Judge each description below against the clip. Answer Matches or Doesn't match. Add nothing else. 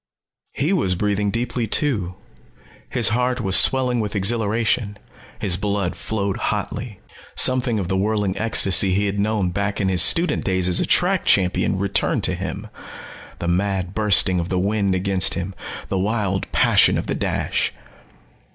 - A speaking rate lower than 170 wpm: Matches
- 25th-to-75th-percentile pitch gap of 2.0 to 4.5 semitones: Matches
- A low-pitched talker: Matches